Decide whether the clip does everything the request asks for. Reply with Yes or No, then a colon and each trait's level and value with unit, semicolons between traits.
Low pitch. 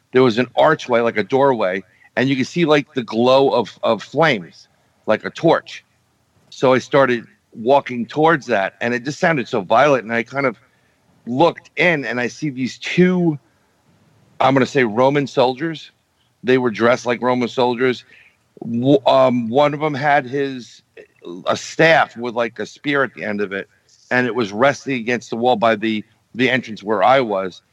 Yes: low, 125 Hz